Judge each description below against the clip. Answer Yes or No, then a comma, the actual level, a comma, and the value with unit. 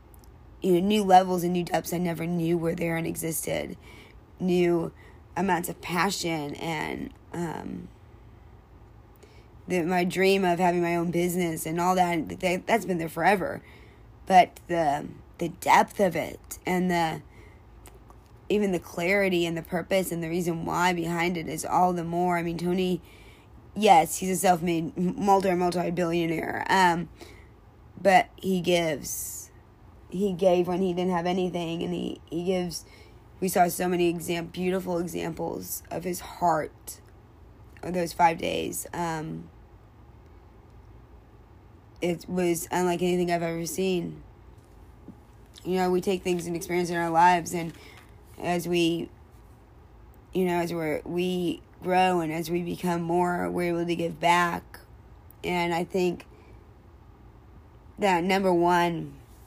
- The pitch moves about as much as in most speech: No, wide, 8.2 semitones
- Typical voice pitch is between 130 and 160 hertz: No, medium, 170 Hz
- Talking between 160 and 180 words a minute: No, average, 140 wpm